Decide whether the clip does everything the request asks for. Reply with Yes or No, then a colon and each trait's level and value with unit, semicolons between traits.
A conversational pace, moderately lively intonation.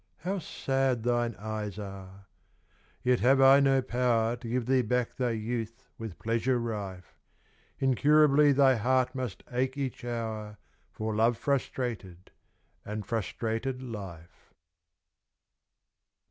No: slow, 120 wpm; average, 3.2 semitones